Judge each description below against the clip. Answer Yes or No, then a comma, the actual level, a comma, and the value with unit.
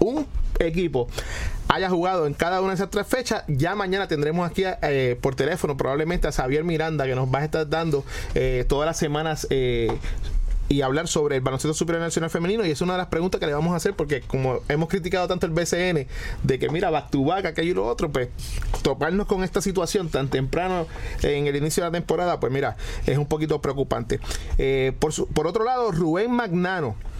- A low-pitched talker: No, medium, 160 Hz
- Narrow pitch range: No, average, 4.6 semitones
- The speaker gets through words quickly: Yes, fast, 210 wpm